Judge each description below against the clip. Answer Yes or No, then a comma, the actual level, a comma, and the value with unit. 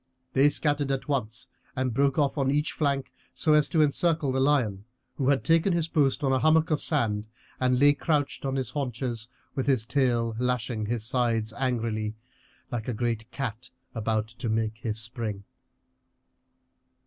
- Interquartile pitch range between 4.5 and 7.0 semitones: No, average, 3.9 semitones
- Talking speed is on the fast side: No, average, 170 wpm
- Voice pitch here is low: Yes, low, 130 Hz